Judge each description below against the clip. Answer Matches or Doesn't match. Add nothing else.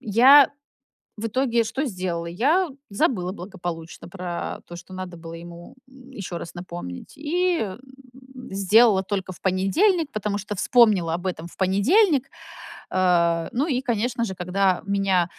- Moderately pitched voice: Doesn't match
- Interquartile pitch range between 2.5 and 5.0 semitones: Doesn't match